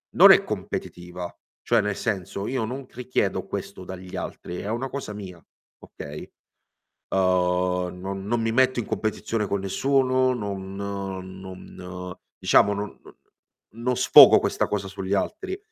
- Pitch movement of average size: Yes, average, 4.1 semitones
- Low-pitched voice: Yes, low, 100 Hz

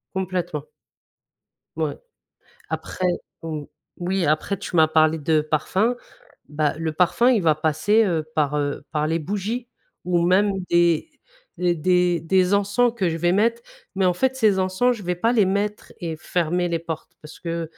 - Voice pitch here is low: No, medium, 175 Hz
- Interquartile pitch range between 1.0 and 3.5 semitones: No, average, 3.9 semitones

